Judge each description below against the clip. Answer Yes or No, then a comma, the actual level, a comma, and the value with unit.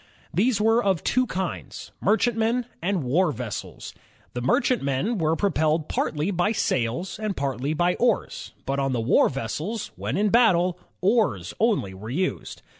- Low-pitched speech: No, medium, 180 Hz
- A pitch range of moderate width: No, wide, 7.6 semitones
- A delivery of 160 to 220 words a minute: No, average, 150 wpm